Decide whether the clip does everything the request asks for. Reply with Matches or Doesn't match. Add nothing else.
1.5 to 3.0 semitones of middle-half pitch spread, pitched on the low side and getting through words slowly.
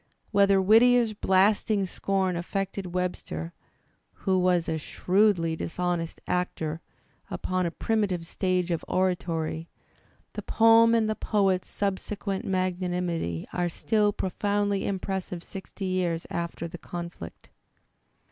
Doesn't match